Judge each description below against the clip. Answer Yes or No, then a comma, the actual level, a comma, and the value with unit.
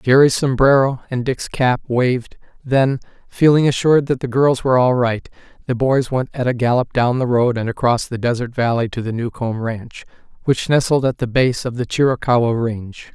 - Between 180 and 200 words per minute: Yes, average, 190 wpm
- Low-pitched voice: Yes, low, 125 Hz